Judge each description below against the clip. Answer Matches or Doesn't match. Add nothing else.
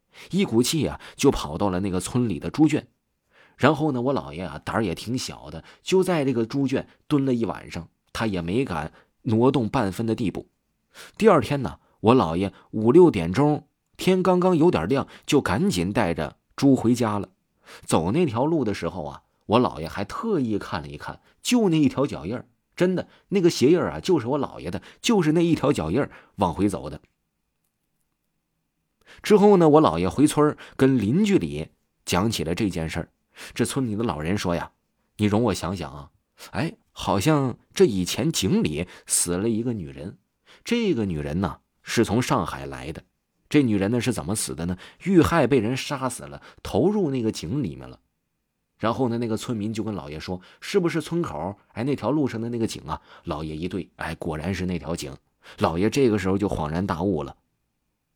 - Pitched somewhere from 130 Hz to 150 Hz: Doesn't match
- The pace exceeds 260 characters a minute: Matches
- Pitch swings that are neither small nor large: Doesn't match